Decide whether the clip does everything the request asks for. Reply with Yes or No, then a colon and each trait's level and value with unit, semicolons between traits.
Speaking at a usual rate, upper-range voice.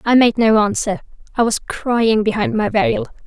Yes: average, 165 wpm; high, 205 Hz